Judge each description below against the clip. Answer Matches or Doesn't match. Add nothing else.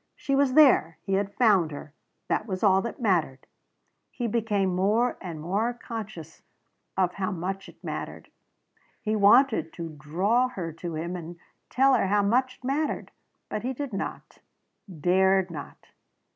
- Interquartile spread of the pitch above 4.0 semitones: Matches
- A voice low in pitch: Doesn't match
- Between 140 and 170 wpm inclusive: Matches